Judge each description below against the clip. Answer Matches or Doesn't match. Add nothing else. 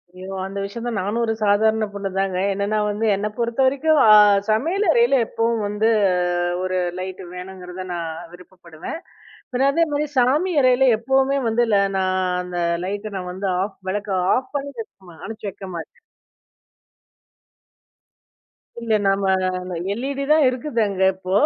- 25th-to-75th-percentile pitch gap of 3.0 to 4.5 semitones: Doesn't match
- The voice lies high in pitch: Matches